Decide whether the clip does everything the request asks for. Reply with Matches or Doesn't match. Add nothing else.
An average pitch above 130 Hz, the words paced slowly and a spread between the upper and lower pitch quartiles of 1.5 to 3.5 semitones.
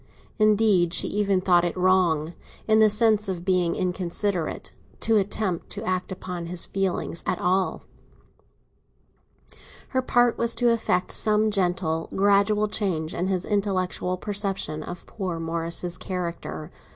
Matches